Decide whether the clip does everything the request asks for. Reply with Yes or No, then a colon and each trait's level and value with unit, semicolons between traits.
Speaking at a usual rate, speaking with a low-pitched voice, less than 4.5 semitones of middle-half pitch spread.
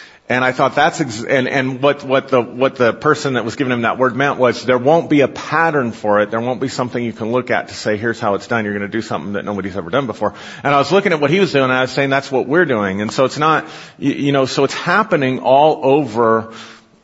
No: fast, 275 wpm; low, 130 Hz; average, 3.7 semitones